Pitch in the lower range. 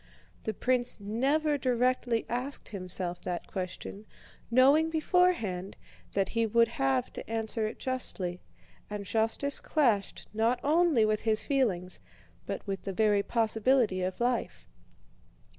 No: high, 225 Hz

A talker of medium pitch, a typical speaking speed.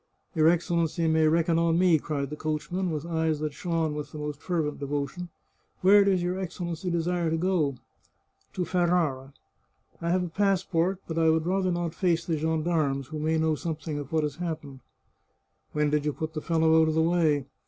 No: medium, 160 Hz; fast, 215 wpm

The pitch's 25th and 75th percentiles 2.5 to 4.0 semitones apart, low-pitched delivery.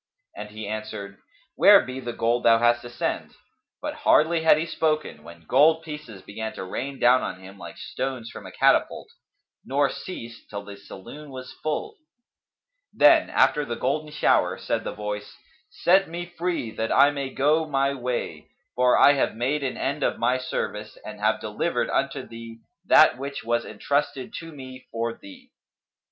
No: average, 5.1 semitones; low, 130 Hz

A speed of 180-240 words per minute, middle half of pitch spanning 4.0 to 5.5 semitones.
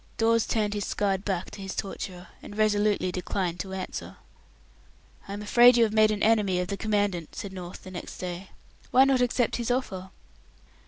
No: average, 190 wpm; average, 2.8 semitones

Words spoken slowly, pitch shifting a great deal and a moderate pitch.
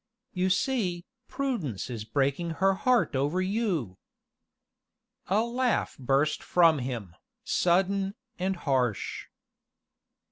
Yes: slow, 100 wpm; wide, 6.4 semitones; medium, 175 Hz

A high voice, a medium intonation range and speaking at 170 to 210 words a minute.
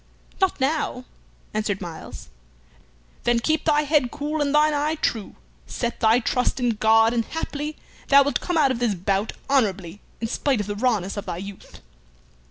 No: high, 240 Hz; wide, 5.9 semitones; average, 175 wpm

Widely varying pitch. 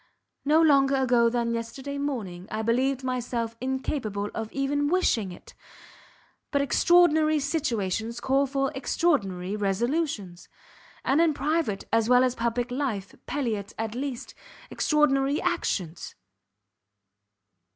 No: average, 4.1 semitones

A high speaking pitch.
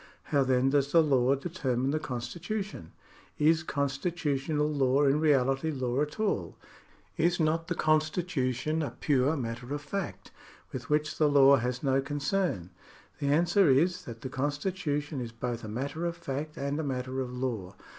No: medium, 140 Hz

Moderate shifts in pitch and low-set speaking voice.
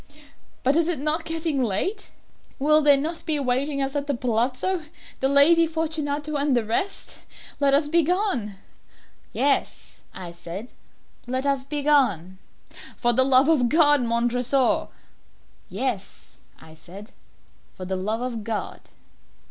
No: average, 4.5 semitones; very high, 275 Hz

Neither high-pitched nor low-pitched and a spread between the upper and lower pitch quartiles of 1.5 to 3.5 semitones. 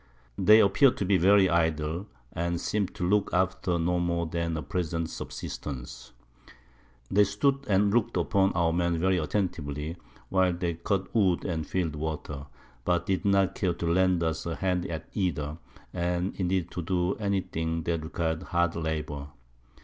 No: very low, 85 Hz; narrow, 2.6 semitones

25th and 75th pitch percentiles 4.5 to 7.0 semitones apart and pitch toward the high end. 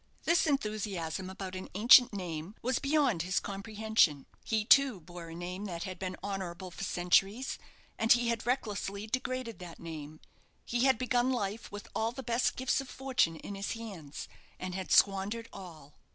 Yes: average, 4.8 semitones; high, 200 Hz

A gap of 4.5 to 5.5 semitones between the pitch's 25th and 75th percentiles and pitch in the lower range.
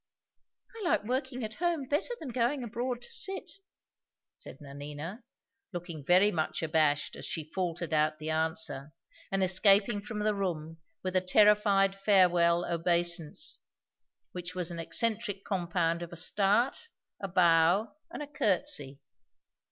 No: average, 4.8 semitones; medium, 185 Hz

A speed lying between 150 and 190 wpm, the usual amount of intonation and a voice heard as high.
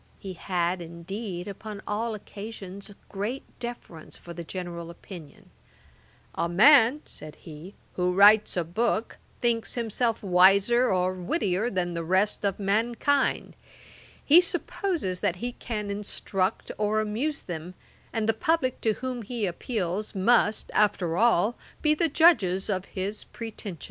No: average, 140 wpm; average, 4.4 semitones; high, 205 Hz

